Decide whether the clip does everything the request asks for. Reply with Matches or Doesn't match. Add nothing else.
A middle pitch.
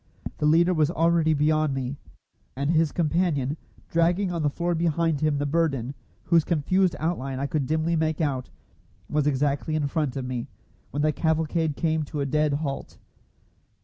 Matches